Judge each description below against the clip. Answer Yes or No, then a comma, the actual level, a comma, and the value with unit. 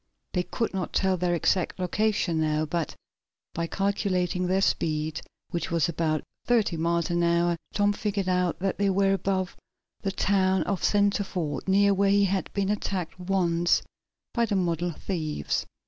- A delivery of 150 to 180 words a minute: Yes, average, 160 wpm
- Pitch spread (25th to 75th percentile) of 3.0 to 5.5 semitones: No, narrow, 2.6 semitones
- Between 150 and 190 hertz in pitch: Yes, medium, 185 Hz